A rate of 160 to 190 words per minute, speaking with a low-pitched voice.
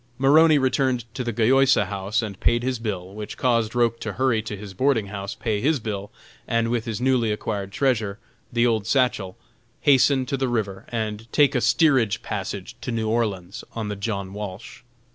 Yes: average, 185 wpm; low, 115 Hz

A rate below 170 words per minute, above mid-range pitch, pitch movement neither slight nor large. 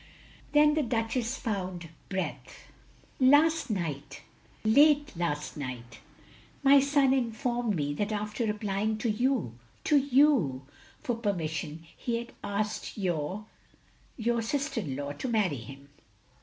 No: slow, 135 wpm; high, 215 Hz; wide, 7.6 semitones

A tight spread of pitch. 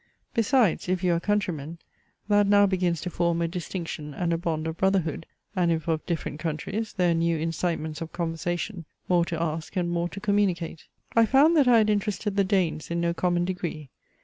No: average, 3.1 semitones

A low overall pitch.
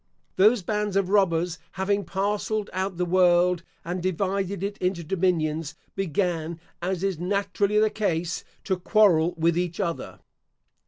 No: medium, 185 Hz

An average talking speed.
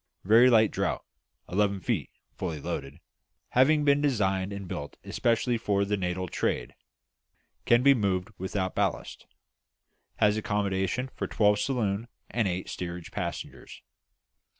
No: slow, 125 wpm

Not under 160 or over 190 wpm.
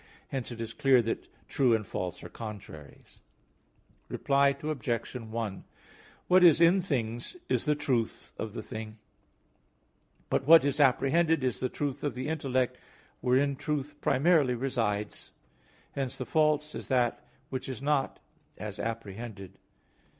No: average, 140 wpm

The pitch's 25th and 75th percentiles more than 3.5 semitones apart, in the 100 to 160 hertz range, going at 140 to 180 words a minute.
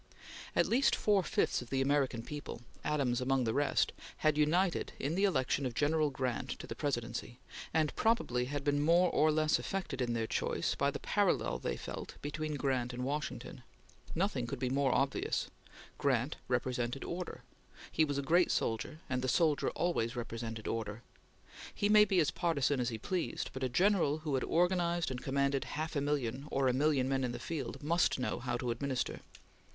No: average, 3.9 semitones; medium, 140 Hz; average, 190 wpm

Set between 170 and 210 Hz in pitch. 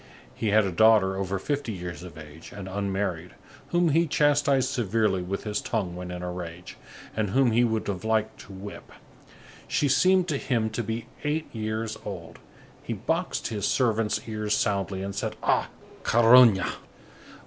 No: low, 105 Hz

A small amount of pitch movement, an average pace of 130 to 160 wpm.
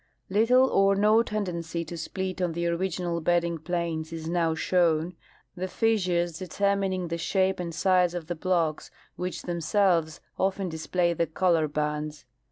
Yes: narrow, 2.3 semitones; average, 150 wpm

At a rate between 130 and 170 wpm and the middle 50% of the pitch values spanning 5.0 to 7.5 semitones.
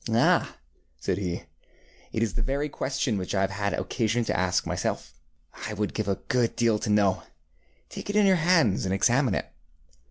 No: average, 195 wpm; wide, 5.4 semitones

